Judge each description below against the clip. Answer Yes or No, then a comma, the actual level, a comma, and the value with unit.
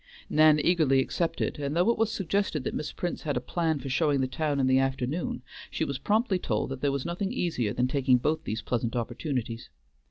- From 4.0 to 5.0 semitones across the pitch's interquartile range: Yes, average, 4.6 semitones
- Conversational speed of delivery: No, fast, 215 wpm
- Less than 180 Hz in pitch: Yes, medium, 140 Hz